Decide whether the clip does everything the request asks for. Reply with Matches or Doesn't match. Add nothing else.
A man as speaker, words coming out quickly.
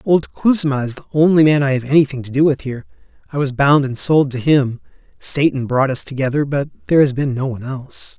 Matches